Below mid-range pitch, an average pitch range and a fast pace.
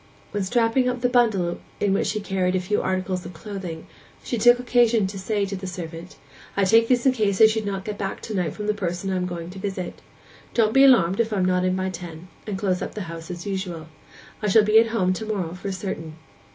No: high, 195 Hz; average, 3.1 semitones; fast, 245 wpm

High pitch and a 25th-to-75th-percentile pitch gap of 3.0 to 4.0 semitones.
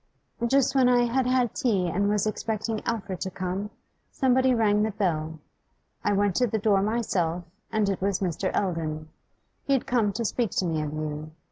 No: high, 205 Hz; average, 4.5 semitones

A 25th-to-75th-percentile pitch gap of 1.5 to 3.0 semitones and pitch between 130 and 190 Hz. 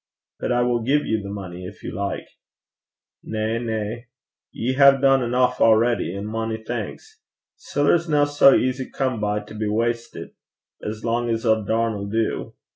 No: average, 2.7 semitones; low, 115 Hz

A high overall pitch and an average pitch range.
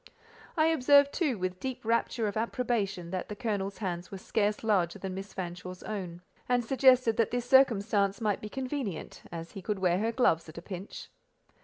Yes: high, 210 Hz; average, 4.8 semitones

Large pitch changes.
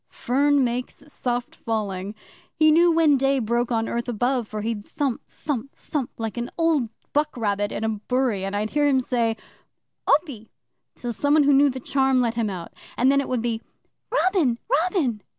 No: average, 4.1 semitones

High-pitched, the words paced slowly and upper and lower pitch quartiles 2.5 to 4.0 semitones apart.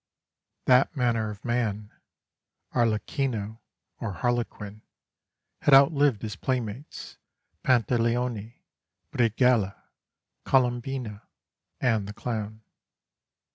No: low, 115 Hz; slow, 75 wpm; average, 2.8 semitones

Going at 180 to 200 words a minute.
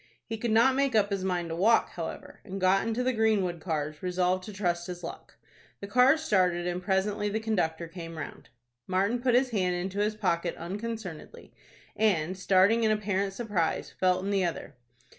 Yes: average, 185 wpm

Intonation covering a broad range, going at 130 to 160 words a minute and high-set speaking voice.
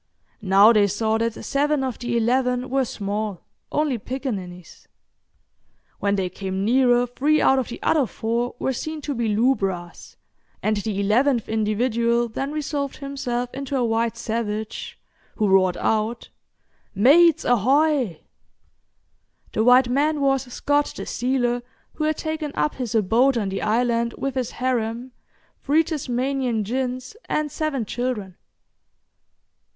No: average, 3.8 semitones; slow, 135 wpm; high, 245 Hz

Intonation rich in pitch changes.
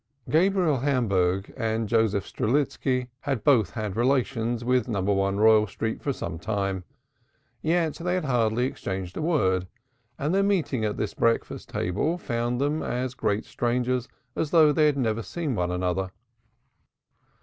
Yes: wide, 5.7 semitones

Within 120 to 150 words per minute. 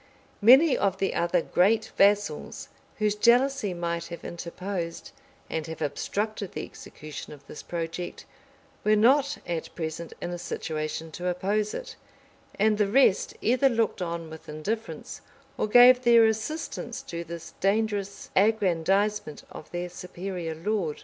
Yes: average, 140 wpm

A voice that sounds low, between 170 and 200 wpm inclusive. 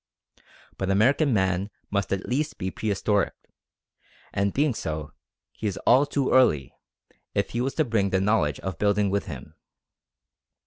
No: low, 100 Hz; average, 150 wpm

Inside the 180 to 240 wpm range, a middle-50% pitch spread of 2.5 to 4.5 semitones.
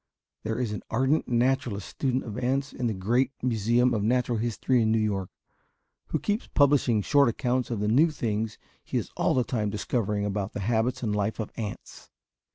Yes: average, 190 wpm; average, 3.2 semitones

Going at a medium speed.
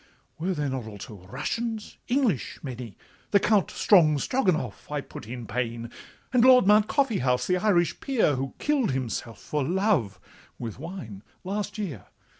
Yes: average, 145 wpm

